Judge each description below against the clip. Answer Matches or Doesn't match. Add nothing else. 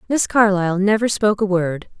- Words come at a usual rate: Matches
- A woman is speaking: Matches